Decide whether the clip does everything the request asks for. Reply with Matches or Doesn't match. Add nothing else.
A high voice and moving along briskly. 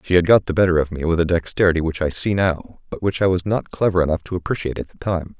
Doesn't match